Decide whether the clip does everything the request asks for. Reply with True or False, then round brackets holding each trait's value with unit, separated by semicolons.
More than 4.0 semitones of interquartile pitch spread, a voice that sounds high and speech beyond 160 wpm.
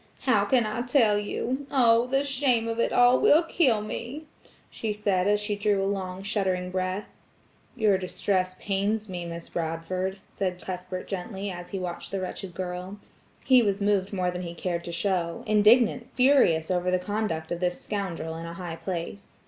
False (3.5 semitones; 195 Hz; 175 wpm)